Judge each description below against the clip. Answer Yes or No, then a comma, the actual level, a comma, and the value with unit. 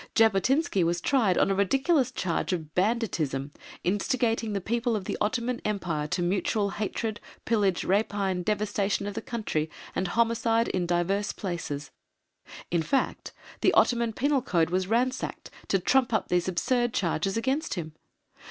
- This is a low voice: No, high, 205 Hz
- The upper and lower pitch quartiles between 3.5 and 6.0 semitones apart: Yes, average, 4.7 semitones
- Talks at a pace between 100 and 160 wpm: Yes, average, 150 wpm